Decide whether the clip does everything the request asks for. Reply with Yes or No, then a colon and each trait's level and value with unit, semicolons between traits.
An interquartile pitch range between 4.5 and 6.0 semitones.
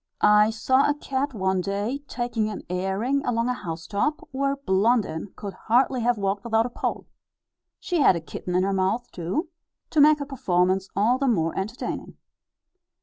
Yes: wide, 5.4 semitones